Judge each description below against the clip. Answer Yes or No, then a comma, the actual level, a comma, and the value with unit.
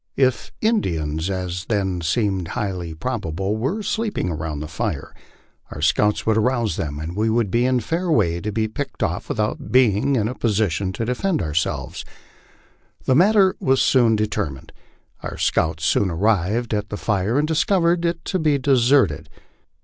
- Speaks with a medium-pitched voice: No, low, 110 Hz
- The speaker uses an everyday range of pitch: No, wide, 6.6 semitones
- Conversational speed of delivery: Yes, average, 165 wpm